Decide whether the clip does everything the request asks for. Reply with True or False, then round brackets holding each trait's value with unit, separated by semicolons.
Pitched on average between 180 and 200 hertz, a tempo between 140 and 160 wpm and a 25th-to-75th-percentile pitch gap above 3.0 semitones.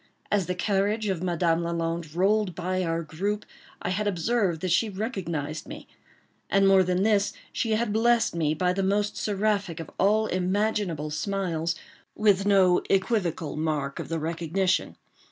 True (185 Hz; 155 wpm; 3.6 semitones)